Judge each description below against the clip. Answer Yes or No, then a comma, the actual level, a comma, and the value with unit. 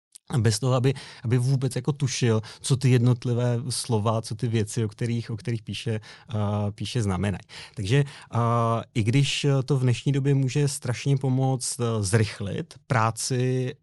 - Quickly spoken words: No, average, 155 wpm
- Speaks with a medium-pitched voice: No, low, 125 Hz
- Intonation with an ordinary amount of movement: Yes, average, 3.1 semitones